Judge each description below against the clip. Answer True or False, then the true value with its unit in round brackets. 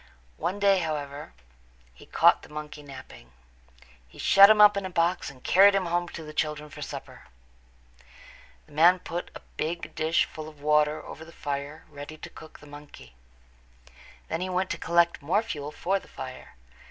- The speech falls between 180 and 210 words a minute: True (185 wpm)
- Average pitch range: True (3.4 semitones)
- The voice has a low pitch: False (155 Hz)